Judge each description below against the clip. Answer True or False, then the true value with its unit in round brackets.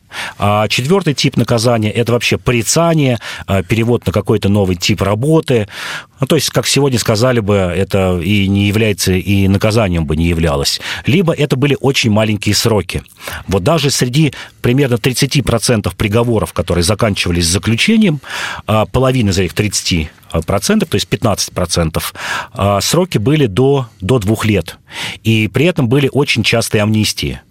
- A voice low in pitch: True (110 Hz)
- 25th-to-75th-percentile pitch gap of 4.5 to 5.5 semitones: True (4.9 semitones)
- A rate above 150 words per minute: False (140 wpm)